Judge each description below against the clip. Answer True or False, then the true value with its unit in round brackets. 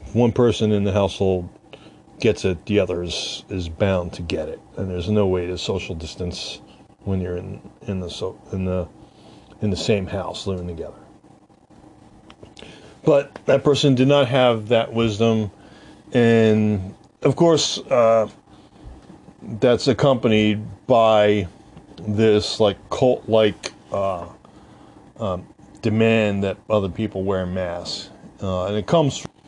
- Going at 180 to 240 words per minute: False (135 wpm)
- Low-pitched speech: True (105 Hz)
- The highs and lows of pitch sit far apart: False (3.3 semitones)